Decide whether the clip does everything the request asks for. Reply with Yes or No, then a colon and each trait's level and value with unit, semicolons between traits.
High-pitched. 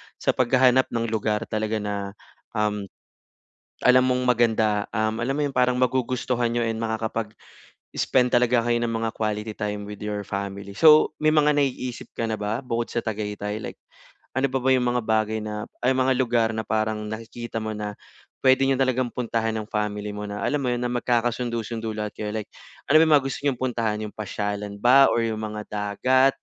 No: low, 115 Hz